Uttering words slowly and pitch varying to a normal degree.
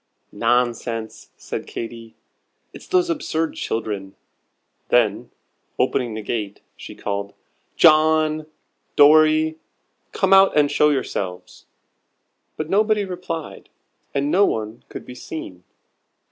No: slow, 105 wpm; wide, 6.1 semitones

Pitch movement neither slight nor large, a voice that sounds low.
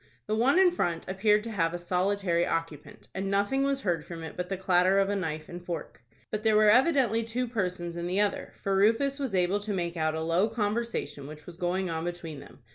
No: average, 4.0 semitones; high, 190 Hz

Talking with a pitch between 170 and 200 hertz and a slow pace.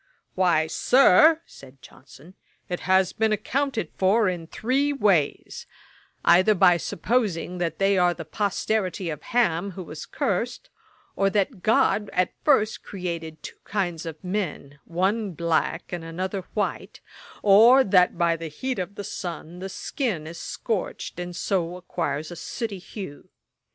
No: medium, 185 Hz; average, 145 wpm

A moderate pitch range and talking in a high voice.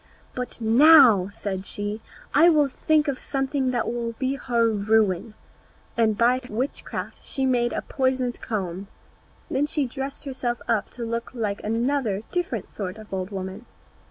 Yes: average, 4.0 semitones; high, 235 Hz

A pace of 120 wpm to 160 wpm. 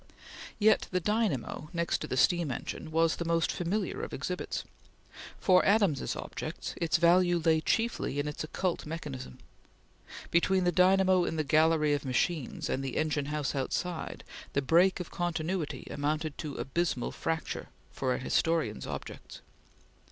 Yes: average, 150 wpm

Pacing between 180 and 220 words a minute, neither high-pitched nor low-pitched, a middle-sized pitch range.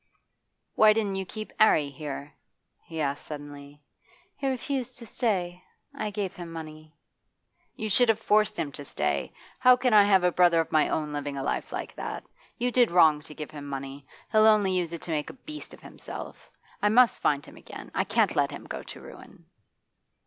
No: average, 200 wpm; medium, 175 Hz; wide, 6.4 semitones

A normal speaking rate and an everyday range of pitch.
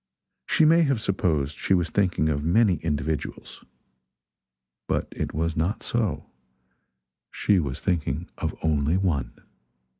No: slow, 125 wpm; average, 4.5 semitones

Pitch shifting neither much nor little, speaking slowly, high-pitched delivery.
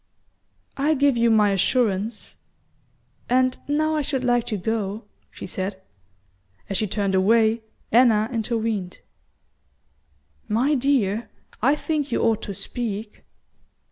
Yes: average, 3.7 semitones; slow, 120 wpm; high, 225 Hz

